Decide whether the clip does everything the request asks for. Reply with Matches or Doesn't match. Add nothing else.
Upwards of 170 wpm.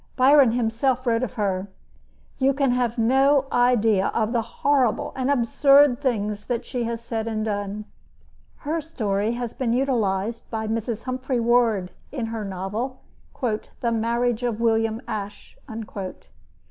Doesn't match